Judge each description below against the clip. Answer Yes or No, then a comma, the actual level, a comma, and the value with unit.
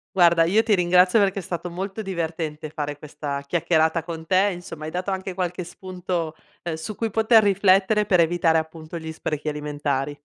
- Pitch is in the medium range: Yes, medium, 175 Hz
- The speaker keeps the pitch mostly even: No, average, 3.1 semitones